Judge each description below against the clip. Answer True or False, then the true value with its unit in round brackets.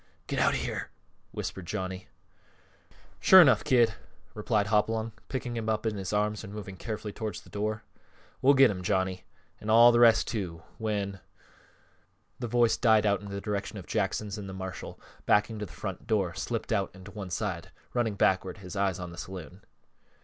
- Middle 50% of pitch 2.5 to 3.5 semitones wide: True (2.8 semitones)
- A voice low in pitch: True (105 Hz)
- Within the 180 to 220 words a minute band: True (200 wpm)